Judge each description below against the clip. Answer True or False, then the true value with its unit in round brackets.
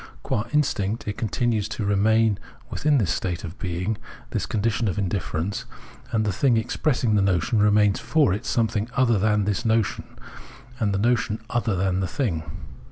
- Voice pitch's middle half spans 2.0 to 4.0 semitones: True (2.8 semitones)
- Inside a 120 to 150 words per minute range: False (170 wpm)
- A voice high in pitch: False (105 Hz)